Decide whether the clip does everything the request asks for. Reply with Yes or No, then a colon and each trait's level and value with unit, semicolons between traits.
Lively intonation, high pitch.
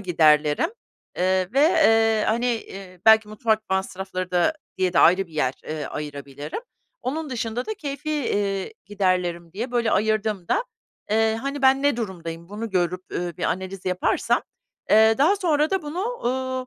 Yes: wide, 6.1 semitones; high, 215 Hz